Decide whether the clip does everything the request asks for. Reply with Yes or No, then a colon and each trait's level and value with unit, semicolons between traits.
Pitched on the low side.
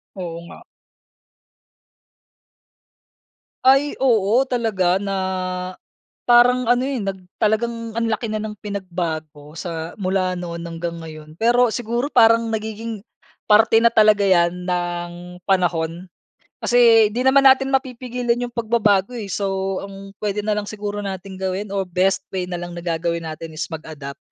No: high, 200 Hz